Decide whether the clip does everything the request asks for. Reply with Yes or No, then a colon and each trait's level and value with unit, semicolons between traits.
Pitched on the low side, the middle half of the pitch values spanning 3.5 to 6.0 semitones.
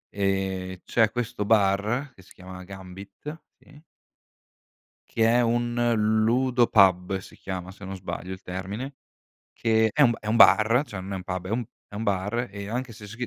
Yes: low, 105 Hz; average, 3.9 semitones